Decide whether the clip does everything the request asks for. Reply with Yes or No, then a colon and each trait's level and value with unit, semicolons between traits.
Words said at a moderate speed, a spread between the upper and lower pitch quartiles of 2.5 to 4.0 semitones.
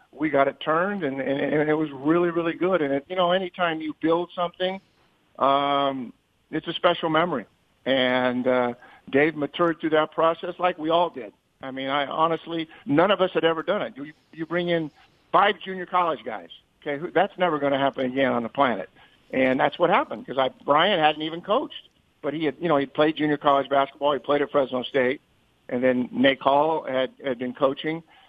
No: fast, 210 wpm; average, 3.6 semitones